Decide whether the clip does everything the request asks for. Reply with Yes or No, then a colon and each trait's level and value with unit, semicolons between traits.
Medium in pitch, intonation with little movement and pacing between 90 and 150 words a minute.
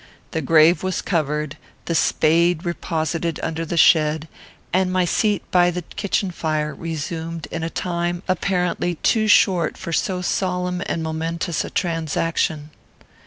Yes: medium, 170 Hz; narrow, 2.1 semitones; average, 140 wpm